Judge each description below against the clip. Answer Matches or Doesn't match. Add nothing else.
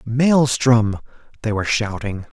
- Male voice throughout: Matches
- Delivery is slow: Matches